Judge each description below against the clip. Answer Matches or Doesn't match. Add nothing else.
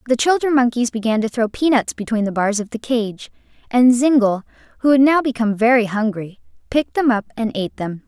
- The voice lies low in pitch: Doesn't match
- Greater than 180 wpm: Matches